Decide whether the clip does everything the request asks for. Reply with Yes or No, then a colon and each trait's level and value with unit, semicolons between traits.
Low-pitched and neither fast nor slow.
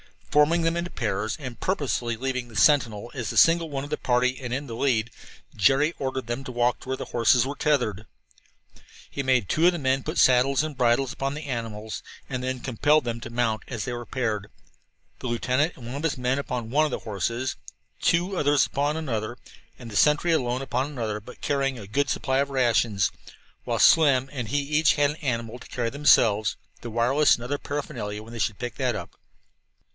No: low, 130 Hz; fast, 210 wpm